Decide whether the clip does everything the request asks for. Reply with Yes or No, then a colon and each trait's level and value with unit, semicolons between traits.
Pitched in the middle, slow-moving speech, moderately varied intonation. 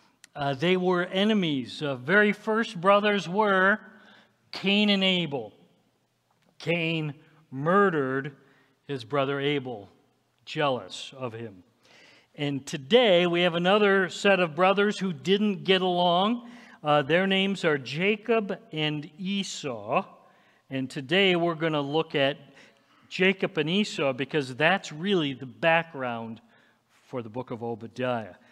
No: medium, 170 Hz; slow, 125 wpm; wide, 5.7 semitones